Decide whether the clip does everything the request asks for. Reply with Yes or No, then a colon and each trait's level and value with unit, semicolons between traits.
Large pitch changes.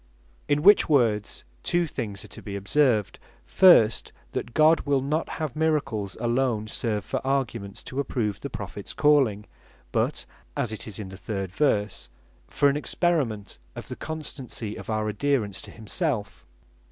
Yes: wide, 5.8 semitones